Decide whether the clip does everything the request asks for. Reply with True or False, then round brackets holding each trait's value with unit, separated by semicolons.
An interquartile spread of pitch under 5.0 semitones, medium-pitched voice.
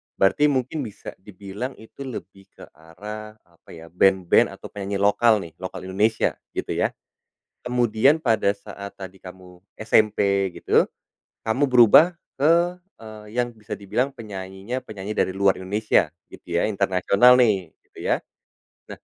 False (3.6 semitones; 105 Hz)